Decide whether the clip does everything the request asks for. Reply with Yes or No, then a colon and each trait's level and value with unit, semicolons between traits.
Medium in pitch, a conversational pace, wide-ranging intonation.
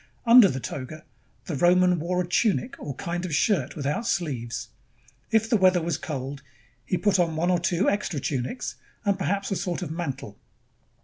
No: medium, 175 Hz; average, 180 wpm; average, 4.7 semitones